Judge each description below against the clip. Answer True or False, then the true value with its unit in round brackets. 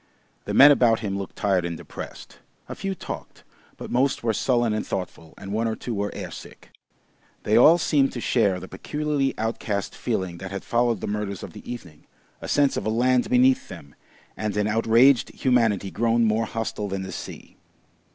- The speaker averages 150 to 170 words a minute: False (190 wpm)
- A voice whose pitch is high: False (110 Hz)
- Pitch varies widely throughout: False (4.0 semitones)